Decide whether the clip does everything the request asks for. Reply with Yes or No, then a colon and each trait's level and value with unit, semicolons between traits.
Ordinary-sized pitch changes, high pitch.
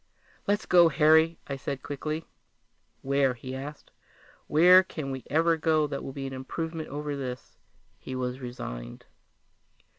No: average, 3.4 semitones; medium, 145 Hz